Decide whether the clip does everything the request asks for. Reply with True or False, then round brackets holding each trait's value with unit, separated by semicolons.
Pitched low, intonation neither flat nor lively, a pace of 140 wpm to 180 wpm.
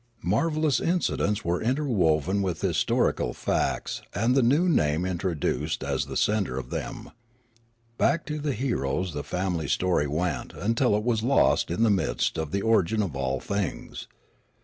False (100 Hz; 6.6 semitones; 155 wpm)